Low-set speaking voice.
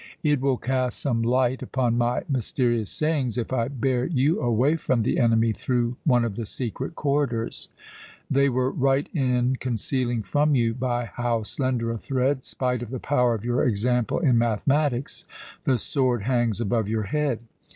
Yes: low, 125 Hz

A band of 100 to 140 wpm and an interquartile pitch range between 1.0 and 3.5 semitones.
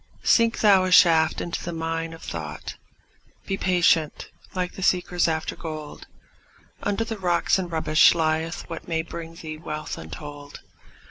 No: average, 150 wpm; narrow, 2.4 semitones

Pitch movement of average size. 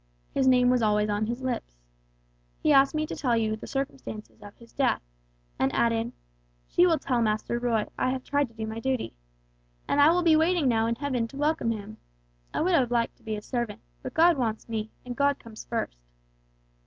Yes: average, 3.9 semitones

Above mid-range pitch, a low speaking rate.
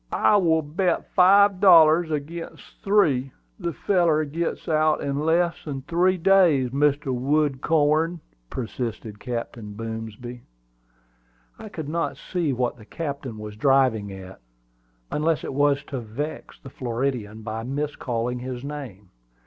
No: medium, 140 Hz; slow, 130 wpm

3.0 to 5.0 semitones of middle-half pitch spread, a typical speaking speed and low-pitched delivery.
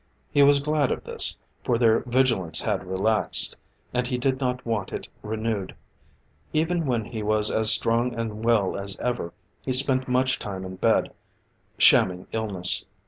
Yes: average, 3.6 semitones; average, 160 wpm; low, 115 Hz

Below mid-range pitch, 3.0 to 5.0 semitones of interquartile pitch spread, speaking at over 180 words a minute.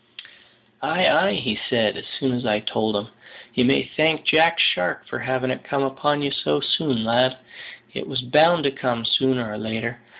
Yes: low, 130 Hz; average, 3.7 semitones; average, 195 wpm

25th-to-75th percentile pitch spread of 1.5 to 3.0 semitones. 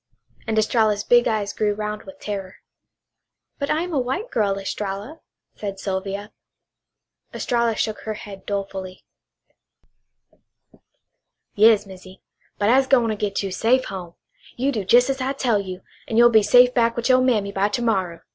No: average, 3.5 semitones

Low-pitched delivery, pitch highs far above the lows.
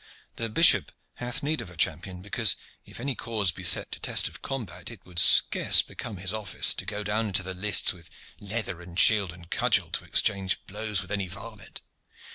No: low, 100 Hz; average, 3.3 semitones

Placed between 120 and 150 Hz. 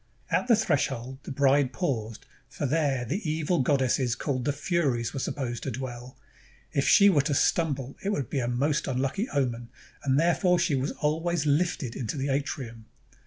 Yes: medium, 140 Hz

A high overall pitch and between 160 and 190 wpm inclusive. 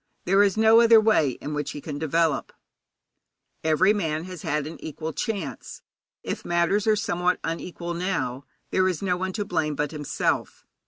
No: medium, 170 Hz; average, 170 wpm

